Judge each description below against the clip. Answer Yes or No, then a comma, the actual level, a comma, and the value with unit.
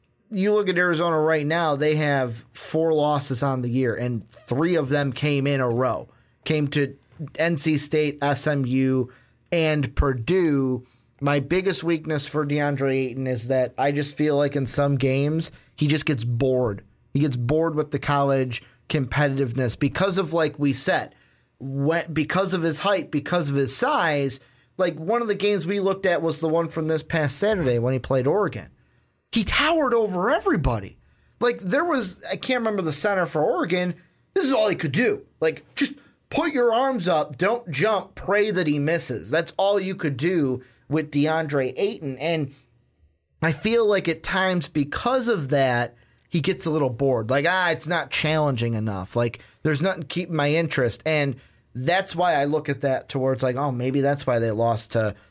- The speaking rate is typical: Yes, average, 180 wpm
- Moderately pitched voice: Yes, medium, 150 Hz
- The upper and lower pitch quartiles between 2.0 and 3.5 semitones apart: No, average, 4.6 semitones